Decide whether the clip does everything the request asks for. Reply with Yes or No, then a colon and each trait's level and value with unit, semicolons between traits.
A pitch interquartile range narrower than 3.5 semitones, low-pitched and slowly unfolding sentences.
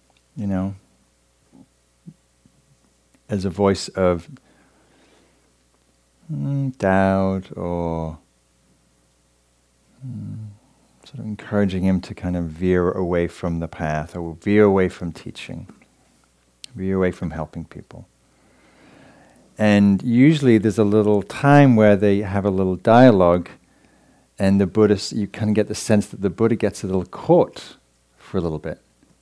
No: wide, 5.4 semitones; very low, 95 Hz; slow, 130 wpm